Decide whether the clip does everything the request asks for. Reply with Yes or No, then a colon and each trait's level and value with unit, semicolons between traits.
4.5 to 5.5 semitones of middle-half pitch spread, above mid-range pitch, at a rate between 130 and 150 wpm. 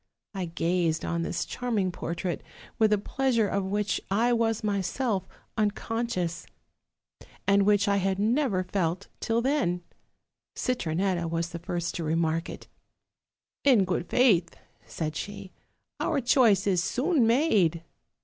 Yes: average, 4.8 semitones; high, 195 Hz; average, 140 wpm